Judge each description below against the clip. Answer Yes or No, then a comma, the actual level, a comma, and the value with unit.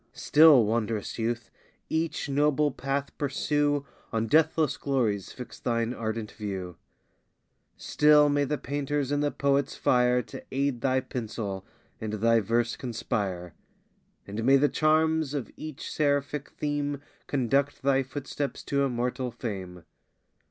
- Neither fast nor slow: No, slow, 130 wpm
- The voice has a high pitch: No, low, 135 Hz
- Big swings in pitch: No, average, 4.0 semitones